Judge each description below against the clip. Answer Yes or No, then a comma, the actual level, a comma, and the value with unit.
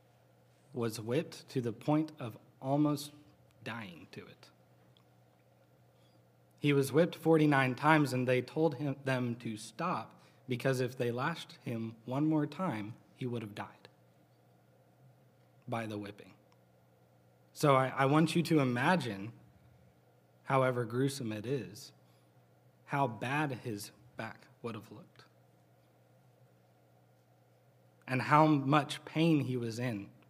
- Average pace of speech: No, slow, 125 wpm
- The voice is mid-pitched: No, low, 120 Hz